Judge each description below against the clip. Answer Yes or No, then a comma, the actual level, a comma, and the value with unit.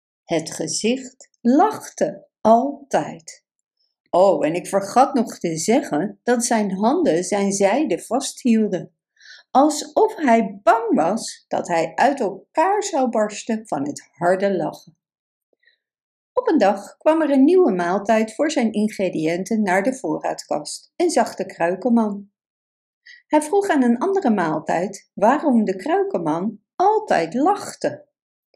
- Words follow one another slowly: Yes, slow, 125 wpm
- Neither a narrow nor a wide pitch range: No, wide, 7.1 semitones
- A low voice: No, high, 230 Hz